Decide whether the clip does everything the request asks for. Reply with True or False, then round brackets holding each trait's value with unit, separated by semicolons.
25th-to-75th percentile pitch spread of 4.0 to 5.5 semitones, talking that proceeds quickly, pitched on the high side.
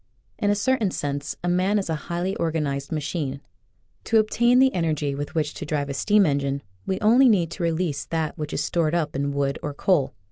False (5.1 semitones; 215 wpm; 160 Hz)